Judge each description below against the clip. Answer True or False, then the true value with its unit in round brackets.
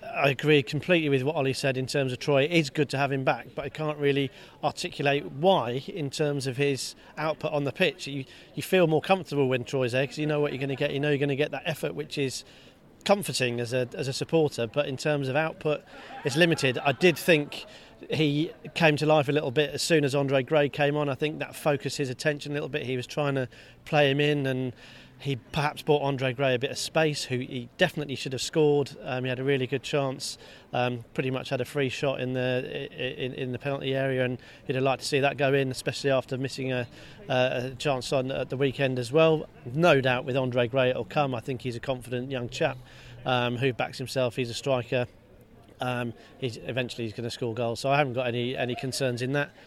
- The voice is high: False (140 Hz)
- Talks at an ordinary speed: False (250 wpm)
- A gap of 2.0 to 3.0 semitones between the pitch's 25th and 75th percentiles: True (2.5 semitones)